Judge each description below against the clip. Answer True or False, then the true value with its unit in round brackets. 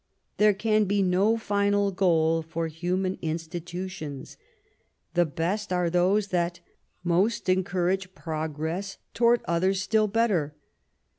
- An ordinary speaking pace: False (115 wpm)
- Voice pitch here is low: False (185 Hz)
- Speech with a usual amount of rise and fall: True (3.3 semitones)